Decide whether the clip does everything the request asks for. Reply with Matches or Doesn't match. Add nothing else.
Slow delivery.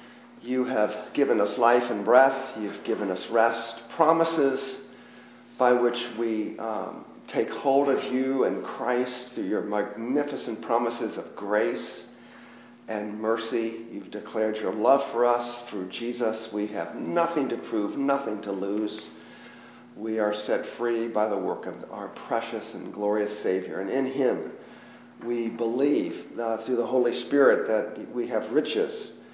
Doesn't match